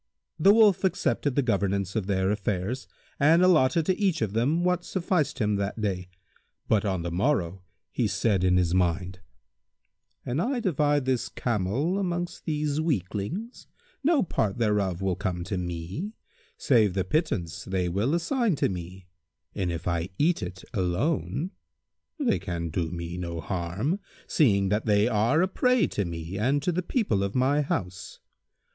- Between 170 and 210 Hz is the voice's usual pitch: No, low, 105 Hz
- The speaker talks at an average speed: Yes, average, 165 wpm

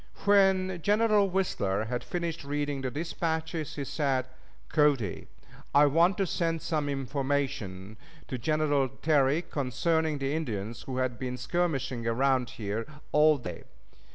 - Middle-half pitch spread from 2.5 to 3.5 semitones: No, average, 4.4 semitones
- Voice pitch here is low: No, medium, 145 Hz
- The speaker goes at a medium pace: No, slow, 130 wpm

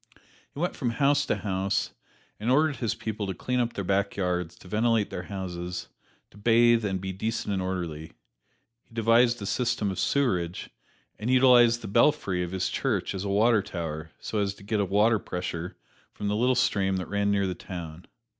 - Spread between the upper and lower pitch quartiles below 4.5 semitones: Yes, average, 4.0 semitones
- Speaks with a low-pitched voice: Yes, low, 100 Hz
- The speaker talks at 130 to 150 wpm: No, average, 195 wpm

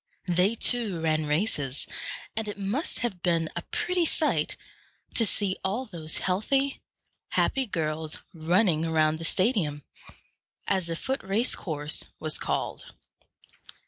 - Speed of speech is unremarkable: No, slow, 130 wpm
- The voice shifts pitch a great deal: Yes, wide, 5.8 semitones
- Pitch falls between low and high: Yes, medium, 180 Hz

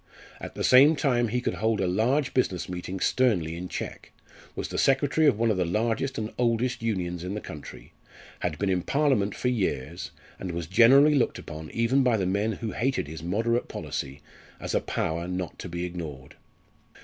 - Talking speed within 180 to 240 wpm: Yes, average, 195 wpm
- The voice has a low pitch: Yes, low, 105 Hz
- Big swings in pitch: Yes, wide, 5.8 semitones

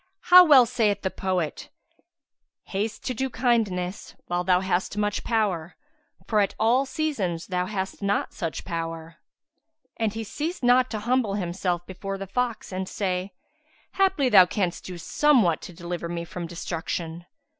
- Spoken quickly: No, average, 155 wpm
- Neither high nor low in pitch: No, high, 195 Hz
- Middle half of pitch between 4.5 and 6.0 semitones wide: Yes, average, 5.0 semitones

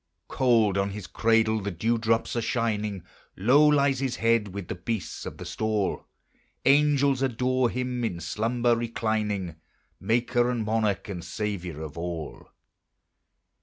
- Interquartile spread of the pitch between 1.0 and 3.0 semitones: No, average, 3.5 semitones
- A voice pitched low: Yes, low, 110 Hz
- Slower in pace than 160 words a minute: Yes, average, 140 wpm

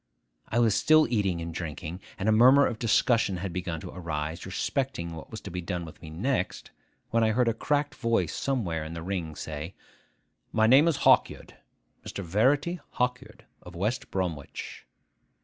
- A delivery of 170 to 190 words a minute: Yes, average, 175 wpm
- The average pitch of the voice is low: Yes, low, 100 Hz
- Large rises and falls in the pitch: Yes, wide, 6.3 semitones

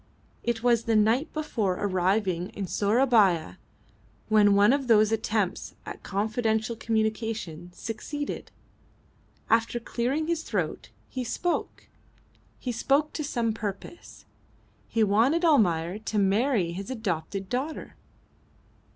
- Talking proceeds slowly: Yes, slow, 115 wpm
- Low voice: No, high, 220 Hz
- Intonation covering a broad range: No, average, 3.7 semitones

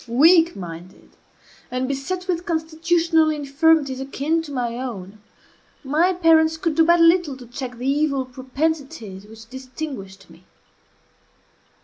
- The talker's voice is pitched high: Yes, very high, 280 Hz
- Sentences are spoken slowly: Yes, slow, 125 wpm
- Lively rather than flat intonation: No, average, 4.4 semitones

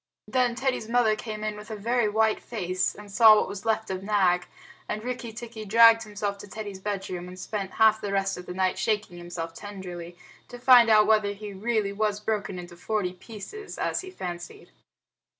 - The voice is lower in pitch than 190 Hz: No, high, 210 Hz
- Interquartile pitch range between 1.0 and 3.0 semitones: Yes, average, 2.7 semitones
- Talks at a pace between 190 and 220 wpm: Yes, average, 195 wpm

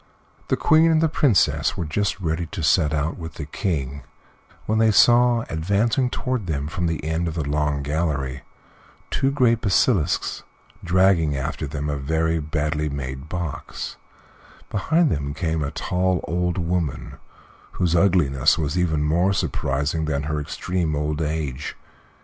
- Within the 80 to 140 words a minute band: No, average, 150 wpm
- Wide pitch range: No, average, 3.9 semitones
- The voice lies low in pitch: Yes, very low, 80 Hz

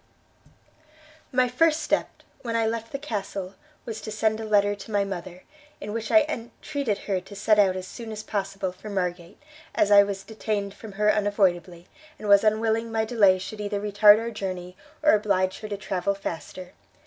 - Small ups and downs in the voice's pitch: Yes, narrow, 2.3 semitones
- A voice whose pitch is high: Yes, high, 205 Hz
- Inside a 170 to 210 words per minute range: Yes, average, 185 wpm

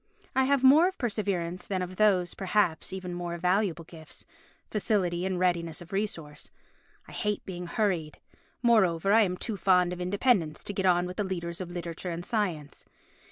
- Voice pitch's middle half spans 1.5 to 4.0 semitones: Yes, average, 3.0 semitones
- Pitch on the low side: No, medium, 180 Hz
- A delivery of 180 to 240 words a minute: No, average, 170 wpm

